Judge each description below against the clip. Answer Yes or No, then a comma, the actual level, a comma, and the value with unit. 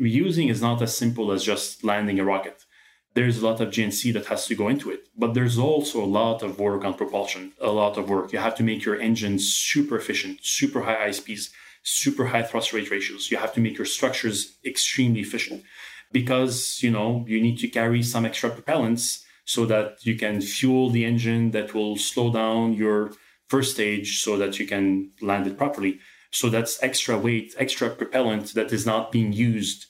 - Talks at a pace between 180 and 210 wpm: Yes, average, 200 wpm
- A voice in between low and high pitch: No, low, 115 Hz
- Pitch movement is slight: Yes, narrow, 2.3 semitones